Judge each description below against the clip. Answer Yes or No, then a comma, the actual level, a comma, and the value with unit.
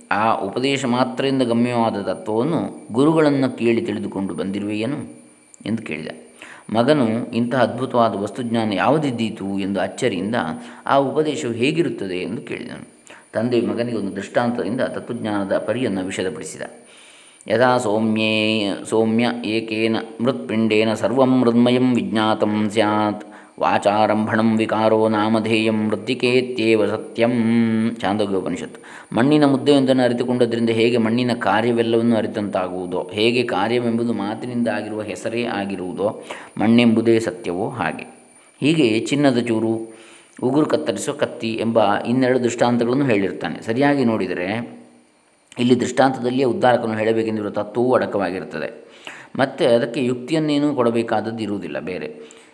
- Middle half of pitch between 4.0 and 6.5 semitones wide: No, narrow, 2.4 semitones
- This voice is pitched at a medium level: No, low, 115 Hz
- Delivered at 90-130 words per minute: Yes, average, 95 wpm